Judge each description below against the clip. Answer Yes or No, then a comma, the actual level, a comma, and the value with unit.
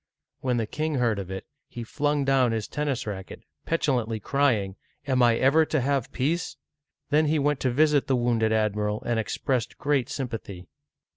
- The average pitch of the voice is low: Yes, low, 125 Hz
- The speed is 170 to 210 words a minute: Yes, average, 175 wpm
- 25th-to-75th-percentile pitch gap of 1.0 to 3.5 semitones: No, average, 4.4 semitones